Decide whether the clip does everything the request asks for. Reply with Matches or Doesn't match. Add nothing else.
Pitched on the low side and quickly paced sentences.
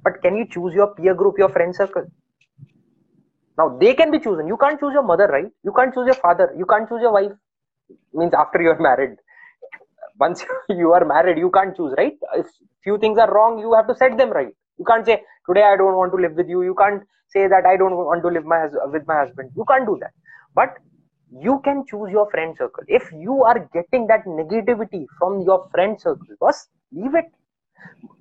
Doesn't match